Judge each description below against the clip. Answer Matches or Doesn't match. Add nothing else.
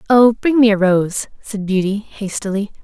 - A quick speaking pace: Doesn't match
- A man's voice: Doesn't match